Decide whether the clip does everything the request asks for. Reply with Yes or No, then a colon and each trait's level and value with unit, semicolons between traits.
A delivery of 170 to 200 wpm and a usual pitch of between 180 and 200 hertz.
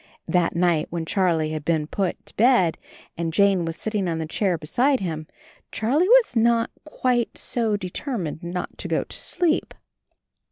Yes: average, 190 wpm; medium, 185 Hz